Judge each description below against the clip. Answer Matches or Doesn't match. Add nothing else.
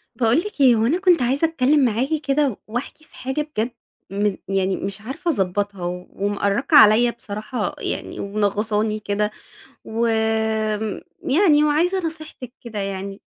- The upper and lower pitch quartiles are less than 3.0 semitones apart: Doesn't match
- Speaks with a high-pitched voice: Matches